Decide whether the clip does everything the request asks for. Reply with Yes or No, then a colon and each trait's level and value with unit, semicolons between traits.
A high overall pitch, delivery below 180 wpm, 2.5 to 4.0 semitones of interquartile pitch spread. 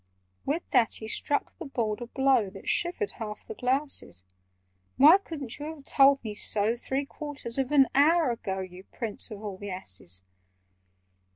No: very high, 250 Hz; average, 170 wpm; wide, 5.4 semitones